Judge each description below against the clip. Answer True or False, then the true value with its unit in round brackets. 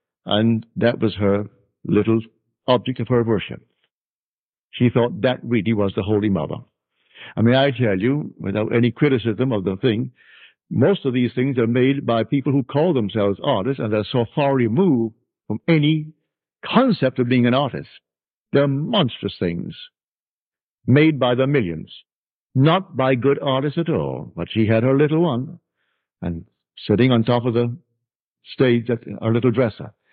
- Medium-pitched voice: False (120 Hz)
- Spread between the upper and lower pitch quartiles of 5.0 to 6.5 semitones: False (3.6 semitones)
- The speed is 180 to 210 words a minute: False (165 wpm)